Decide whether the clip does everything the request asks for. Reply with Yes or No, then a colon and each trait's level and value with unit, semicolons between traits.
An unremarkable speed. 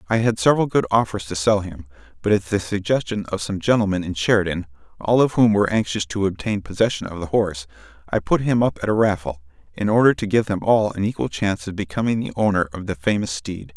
No: fast, 225 wpm